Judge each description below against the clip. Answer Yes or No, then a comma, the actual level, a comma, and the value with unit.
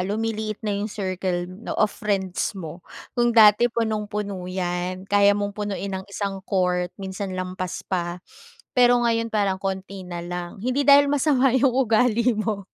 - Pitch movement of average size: Yes, average, 3.3 semitones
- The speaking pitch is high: Yes, high, 200 Hz